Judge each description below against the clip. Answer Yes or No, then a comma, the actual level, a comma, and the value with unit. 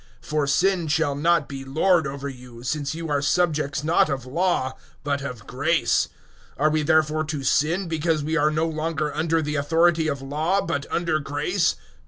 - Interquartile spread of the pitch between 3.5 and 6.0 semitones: No, narrow, 2.6 semitones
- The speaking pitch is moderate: Yes, medium, 155 Hz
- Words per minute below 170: No, average, 190 wpm